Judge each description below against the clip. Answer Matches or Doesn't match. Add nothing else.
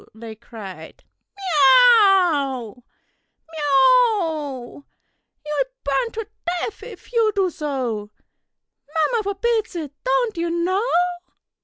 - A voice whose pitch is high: Matches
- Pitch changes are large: Matches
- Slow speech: Matches